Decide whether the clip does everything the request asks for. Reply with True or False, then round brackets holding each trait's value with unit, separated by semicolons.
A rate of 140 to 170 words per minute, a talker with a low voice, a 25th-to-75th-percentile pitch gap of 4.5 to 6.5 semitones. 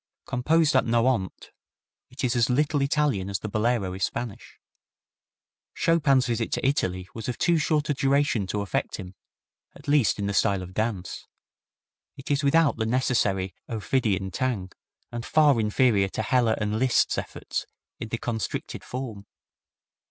True (155 wpm; 120 Hz; 5.1 semitones)